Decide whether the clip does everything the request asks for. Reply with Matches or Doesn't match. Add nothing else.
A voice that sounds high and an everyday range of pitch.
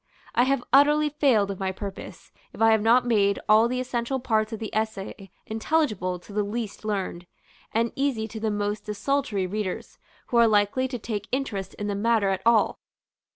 Matches